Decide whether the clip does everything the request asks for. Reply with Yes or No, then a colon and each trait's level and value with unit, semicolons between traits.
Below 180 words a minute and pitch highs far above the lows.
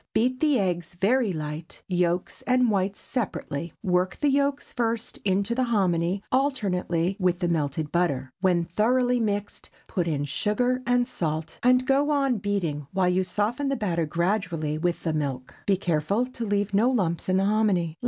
Yes: average, 170 wpm; wide, 5.9 semitones